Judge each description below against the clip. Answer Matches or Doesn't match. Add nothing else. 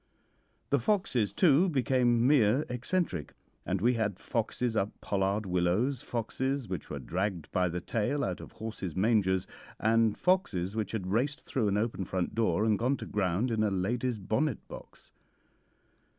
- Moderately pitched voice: Doesn't match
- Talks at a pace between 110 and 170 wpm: Matches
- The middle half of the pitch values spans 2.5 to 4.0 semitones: Doesn't match